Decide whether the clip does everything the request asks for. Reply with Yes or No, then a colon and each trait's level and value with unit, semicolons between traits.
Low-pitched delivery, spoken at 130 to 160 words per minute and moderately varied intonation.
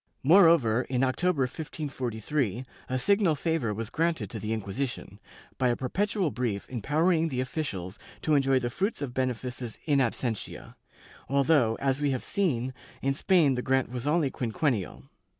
Yes: low, 130 Hz; average, 150 wpm; average, 4.5 semitones